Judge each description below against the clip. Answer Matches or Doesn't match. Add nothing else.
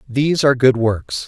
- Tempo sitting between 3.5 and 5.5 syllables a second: Matches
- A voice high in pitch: Doesn't match